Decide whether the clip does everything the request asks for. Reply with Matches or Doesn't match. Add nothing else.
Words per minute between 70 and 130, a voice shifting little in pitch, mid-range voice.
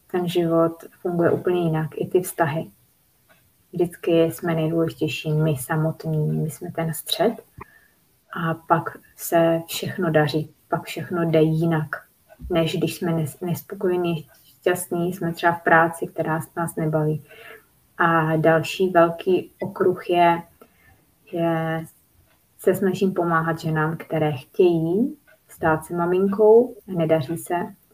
Matches